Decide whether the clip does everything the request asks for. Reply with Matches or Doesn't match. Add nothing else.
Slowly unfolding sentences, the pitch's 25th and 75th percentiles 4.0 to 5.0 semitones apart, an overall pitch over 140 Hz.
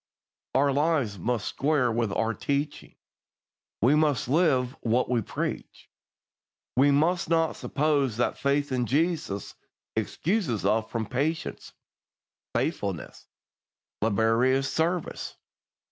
Doesn't match